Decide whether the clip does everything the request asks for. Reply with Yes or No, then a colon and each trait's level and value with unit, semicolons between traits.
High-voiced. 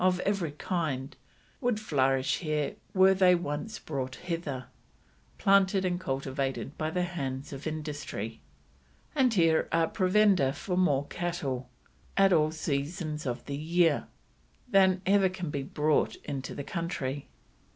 No: medium, 160 Hz